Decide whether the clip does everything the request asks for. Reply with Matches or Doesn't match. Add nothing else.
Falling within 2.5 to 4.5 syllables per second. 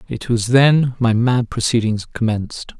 Matches